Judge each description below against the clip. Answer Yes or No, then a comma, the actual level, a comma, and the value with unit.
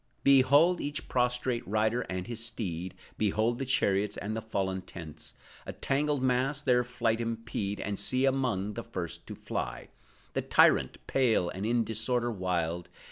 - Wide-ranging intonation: No, average, 4.3 semitones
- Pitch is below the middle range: Yes, low, 115 Hz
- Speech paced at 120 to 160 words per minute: Yes, average, 155 wpm